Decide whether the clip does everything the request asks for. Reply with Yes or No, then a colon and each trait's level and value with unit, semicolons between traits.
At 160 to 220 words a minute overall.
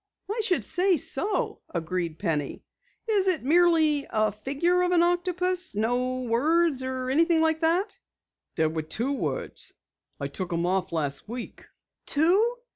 No: average, 145 wpm